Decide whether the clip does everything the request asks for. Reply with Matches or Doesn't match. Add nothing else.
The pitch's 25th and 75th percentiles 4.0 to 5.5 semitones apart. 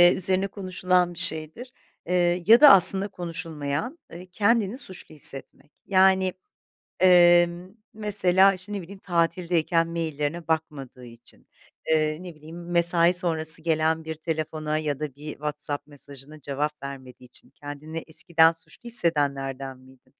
Doesn't match